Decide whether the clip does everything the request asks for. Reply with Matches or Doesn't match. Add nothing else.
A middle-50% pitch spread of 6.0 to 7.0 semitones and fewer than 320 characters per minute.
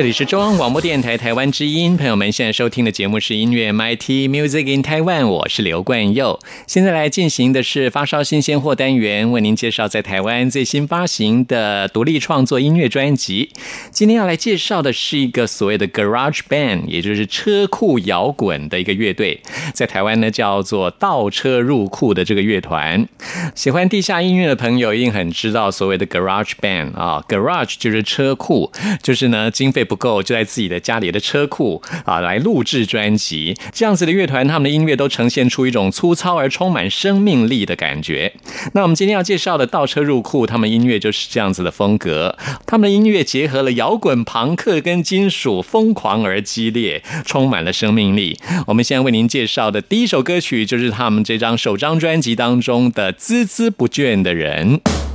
Doesn't match